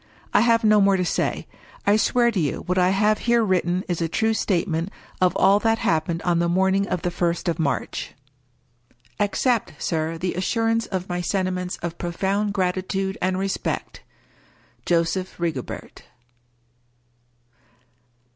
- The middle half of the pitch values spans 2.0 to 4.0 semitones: Yes, average, 2.9 semitones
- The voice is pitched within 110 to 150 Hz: No, medium, 185 Hz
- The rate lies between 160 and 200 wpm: No, average, 145 wpm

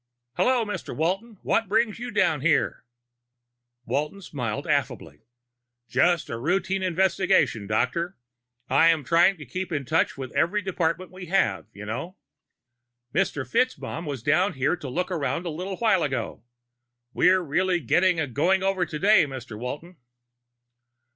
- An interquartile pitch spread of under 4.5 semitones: No, average, 5.2 semitones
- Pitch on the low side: No, medium, 175 Hz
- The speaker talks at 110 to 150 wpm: Yes, average, 140 wpm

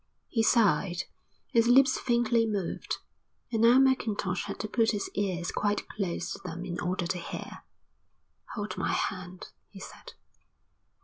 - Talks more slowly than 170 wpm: Yes, average, 145 wpm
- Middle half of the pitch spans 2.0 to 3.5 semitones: No, average, 4.1 semitones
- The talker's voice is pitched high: Yes, high, 205 Hz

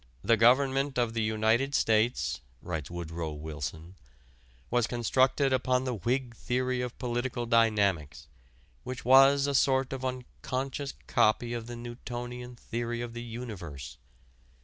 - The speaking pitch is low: Yes, low, 120 Hz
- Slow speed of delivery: Yes, slow, 130 wpm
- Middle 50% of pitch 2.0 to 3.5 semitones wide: Yes, average, 2.9 semitones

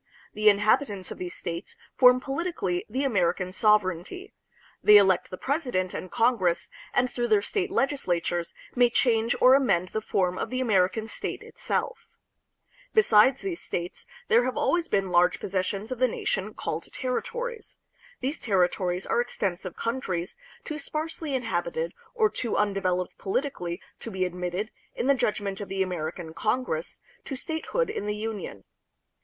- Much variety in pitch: Yes, wide, 6.1 semitones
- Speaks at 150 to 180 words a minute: Yes, average, 155 wpm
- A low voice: No, high, 210 Hz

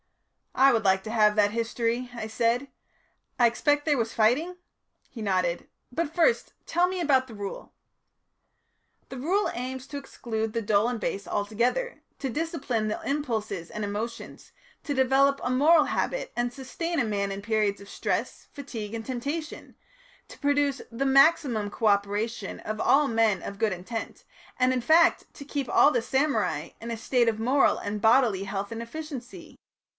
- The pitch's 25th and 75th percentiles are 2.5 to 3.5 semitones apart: No, average, 4.5 semitones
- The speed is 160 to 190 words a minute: Yes, average, 170 wpm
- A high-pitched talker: Yes, high, 235 Hz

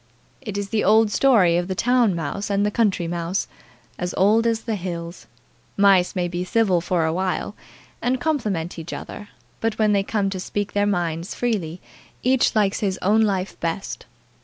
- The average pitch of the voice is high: Yes, high, 195 Hz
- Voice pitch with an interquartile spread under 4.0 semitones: Yes, average, 3.5 semitones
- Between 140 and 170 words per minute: No, average, 180 wpm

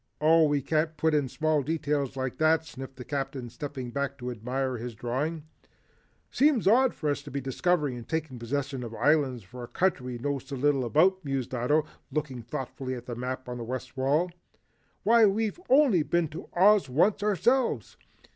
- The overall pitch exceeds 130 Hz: Yes, medium, 140 Hz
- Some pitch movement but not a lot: Yes, average, 4.1 semitones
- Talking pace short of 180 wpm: No, average, 185 wpm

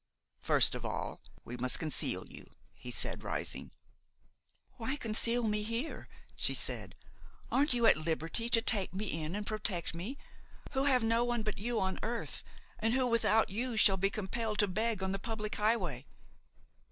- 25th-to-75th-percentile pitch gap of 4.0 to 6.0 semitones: No, average, 3.5 semitones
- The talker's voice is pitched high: Yes, high, 215 Hz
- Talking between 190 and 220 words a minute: No, average, 170 wpm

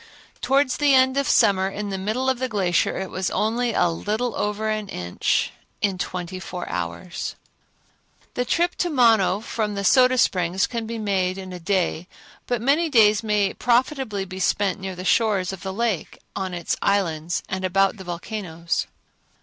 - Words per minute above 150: Yes, average, 180 wpm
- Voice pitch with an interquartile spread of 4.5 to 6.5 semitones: No, average, 4.1 semitones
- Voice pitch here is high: Yes, high, 200 Hz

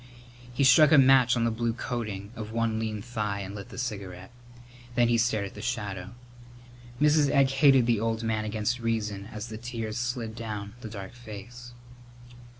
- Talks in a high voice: No, low, 115 Hz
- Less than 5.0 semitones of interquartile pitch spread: Yes, narrow, 2.5 semitones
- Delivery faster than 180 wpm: No, average, 175 wpm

